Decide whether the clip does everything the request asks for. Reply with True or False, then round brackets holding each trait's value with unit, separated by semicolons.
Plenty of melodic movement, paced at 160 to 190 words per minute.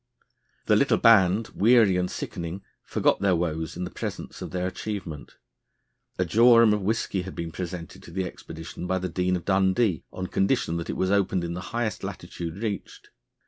False (2.7 semitones; 185 wpm)